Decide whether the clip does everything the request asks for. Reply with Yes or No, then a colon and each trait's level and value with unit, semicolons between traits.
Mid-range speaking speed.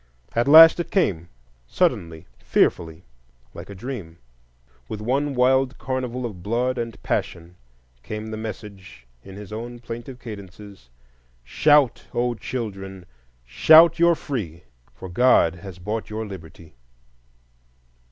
No: slow, 120 wpm